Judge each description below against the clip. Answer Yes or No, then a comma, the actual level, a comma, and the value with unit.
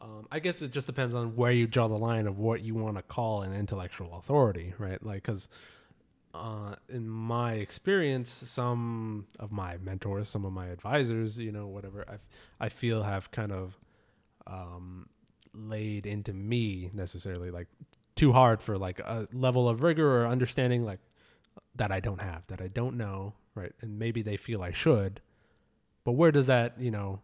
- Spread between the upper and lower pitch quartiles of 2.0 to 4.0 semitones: Yes, average, 3.3 semitones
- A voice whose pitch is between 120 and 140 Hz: No, low, 110 Hz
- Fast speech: No, average, 185 wpm